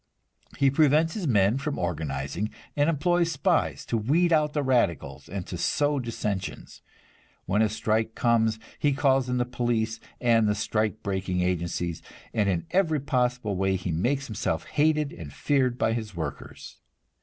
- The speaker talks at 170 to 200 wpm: No, average, 160 wpm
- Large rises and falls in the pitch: Yes, wide, 6.6 semitones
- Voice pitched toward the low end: Yes, low, 115 Hz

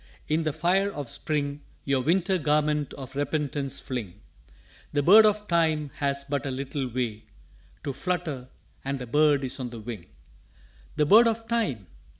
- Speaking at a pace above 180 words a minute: No, average, 160 wpm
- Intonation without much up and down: No, average, 3.9 semitones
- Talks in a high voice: No, medium, 145 Hz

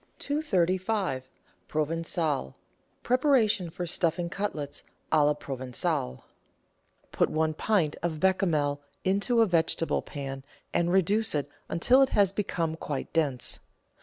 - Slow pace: Yes, slow, 115 wpm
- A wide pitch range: No, average, 4.9 semitones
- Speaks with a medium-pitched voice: Yes, medium, 170 Hz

